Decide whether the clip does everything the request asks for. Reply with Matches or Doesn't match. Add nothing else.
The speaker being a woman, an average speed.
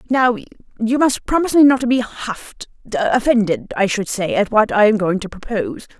Matches